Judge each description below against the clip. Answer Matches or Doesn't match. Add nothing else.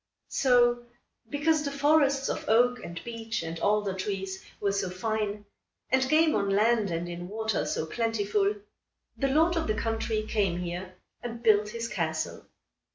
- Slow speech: Doesn't match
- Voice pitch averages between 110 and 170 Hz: Doesn't match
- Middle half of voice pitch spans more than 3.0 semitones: Matches